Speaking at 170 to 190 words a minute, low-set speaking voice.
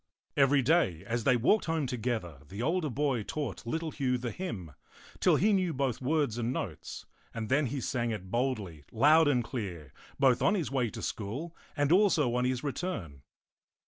Yes: average, 185 wpm; low, 125 Hz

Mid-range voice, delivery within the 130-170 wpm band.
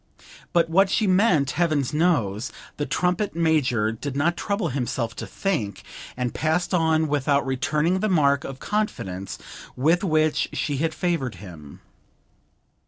Yes: medium, 155 Hz; average, 140 wpm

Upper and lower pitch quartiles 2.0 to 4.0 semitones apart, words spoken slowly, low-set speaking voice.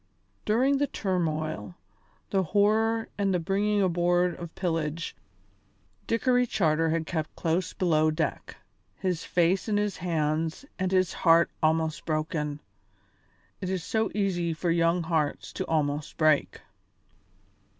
No: average, 3.5 semitones; slow, 130 wpm; medium, 170 Hz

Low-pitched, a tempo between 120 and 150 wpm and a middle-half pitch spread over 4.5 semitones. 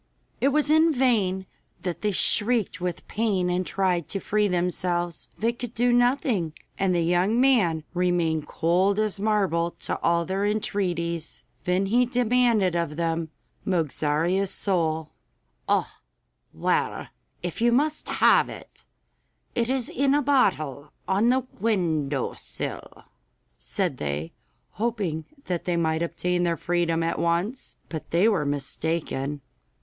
No: medium, 180 Hz; slow, 135 wpm; average, 4.9 semitones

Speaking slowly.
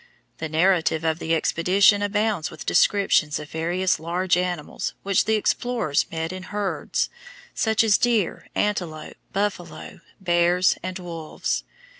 Yes: slow, 130 wpm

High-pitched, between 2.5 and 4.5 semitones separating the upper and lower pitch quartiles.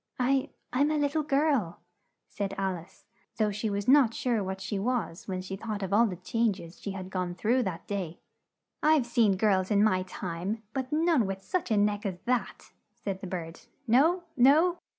No: high, 210 Hz; average, 5.0 semitones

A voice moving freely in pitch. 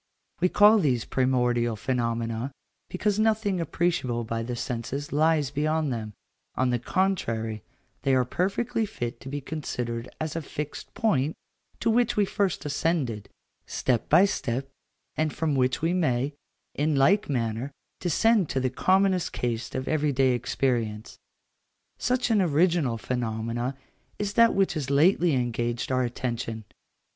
Yes: wide, 6.5 semitones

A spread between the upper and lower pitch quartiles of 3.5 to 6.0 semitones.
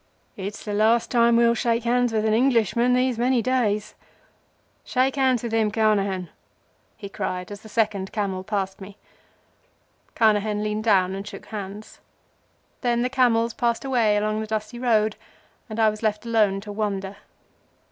No: narrow, 2.4 semitones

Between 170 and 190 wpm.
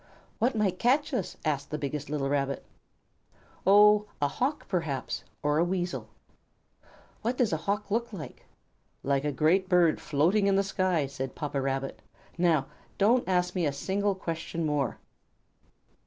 No: average, 155 wpm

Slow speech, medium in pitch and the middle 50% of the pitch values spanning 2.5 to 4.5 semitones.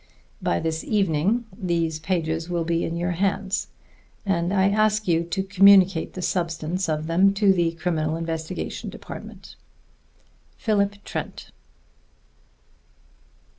Yes: slow, 120 wpm; medium, 175 Hz; average, 3.0 semitones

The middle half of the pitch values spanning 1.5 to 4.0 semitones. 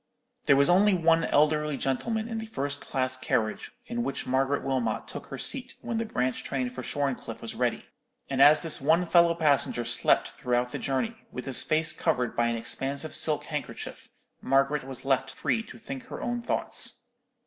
No: average, 4.6 semitones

